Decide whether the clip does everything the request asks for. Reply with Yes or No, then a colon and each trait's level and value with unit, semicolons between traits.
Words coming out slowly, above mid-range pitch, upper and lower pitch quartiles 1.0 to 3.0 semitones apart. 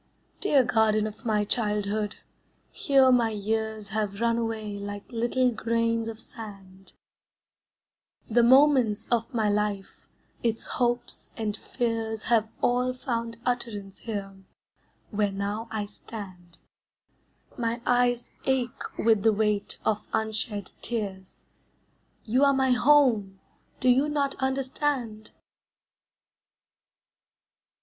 Yes: slow, 110 wpm; high, 225 Hz; average, 2.7 semitones